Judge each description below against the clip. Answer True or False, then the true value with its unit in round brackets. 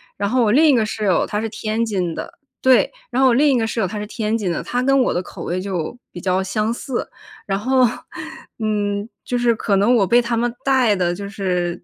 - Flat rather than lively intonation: False (3.6 semitones)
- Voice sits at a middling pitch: False (215 Hz)